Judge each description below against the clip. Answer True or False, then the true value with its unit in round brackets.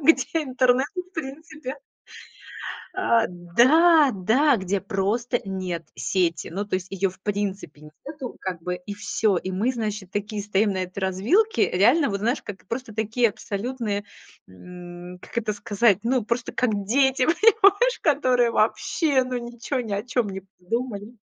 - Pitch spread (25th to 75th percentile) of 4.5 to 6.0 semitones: True (5.1 semitones)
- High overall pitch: True (220 Hz)